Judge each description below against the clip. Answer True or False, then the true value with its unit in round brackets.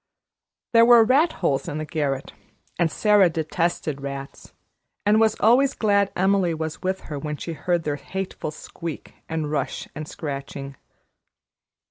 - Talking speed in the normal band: True (145 wpm)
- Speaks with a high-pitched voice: False (165 Hz)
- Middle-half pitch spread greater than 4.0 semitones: True (5.4 semitones)